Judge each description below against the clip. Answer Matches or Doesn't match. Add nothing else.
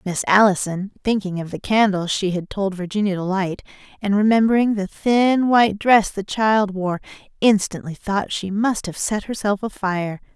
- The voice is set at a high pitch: Matches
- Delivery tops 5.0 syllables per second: Doesn't match